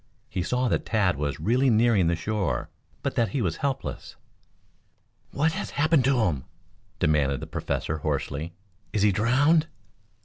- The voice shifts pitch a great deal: Yes, wide, 7.7 semitones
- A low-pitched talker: Yes, low, 110 Hz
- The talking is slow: No, average, 150 wpm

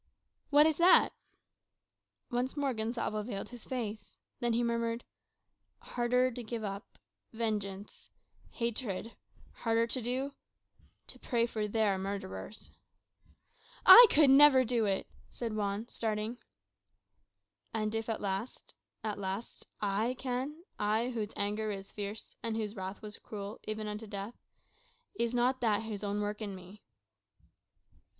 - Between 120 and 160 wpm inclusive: Yes, slow, 135 wpm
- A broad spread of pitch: No, average, 2.7 semitones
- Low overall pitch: No, high, 220 Hz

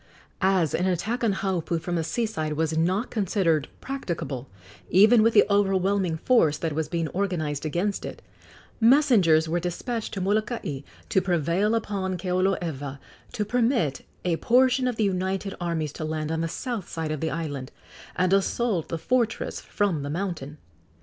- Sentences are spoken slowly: No, average, 165 wpm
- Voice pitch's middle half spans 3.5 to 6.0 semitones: Yes, average, 4.7 semitones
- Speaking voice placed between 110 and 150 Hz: No, medium, 185 Hz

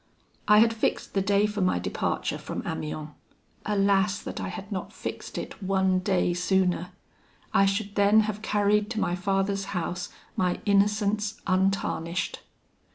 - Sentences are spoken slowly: No, average, 150 wpm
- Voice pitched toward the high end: Yes, high, 195 Hz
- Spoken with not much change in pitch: Yes, narrow, 2.0 semitones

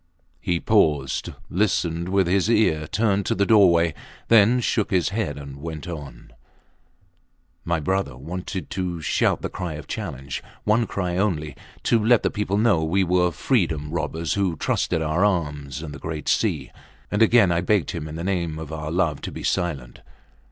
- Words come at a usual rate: Yes, average, 175 wpm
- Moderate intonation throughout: Yes, average, 4.3 semitones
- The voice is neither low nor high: No, very low, 85 Hz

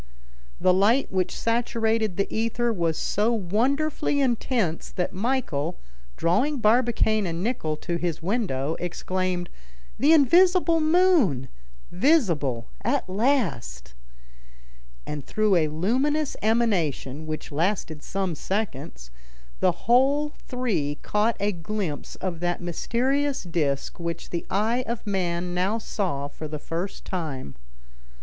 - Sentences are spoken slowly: Yes, slow, 120 wpm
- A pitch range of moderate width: No, wide, 6.3 semitones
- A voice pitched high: Yes, high, 195 Hz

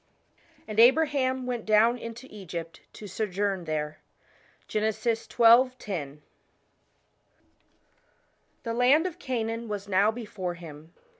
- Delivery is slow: Yes, slow, 105 wpm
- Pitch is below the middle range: No, high, 220 Hz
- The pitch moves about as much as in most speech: Yes, average, 4.5 semitones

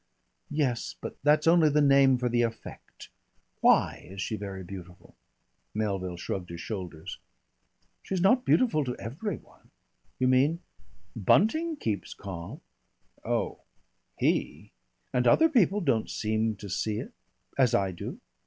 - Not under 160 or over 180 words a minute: No, average, 140 wpm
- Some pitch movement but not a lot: No, wide, 7.7 semitones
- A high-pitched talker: No, low, 120 Hz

